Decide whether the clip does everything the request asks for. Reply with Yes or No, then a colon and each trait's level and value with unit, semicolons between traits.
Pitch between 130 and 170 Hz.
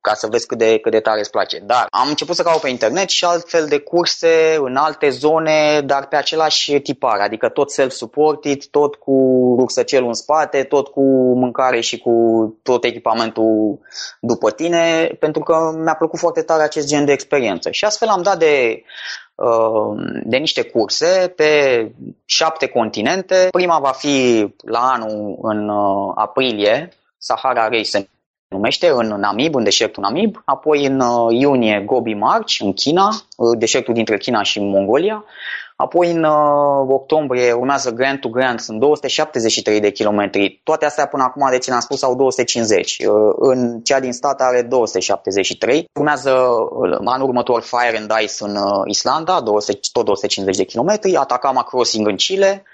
Yes: low, 135 Hz